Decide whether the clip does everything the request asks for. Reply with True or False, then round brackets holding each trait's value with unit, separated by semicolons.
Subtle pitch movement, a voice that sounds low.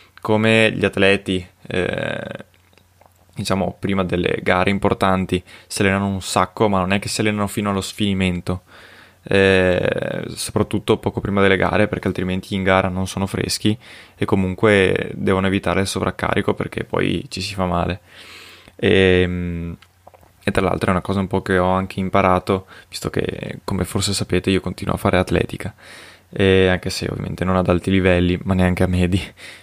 True (1.6 semitones; 95 Hz)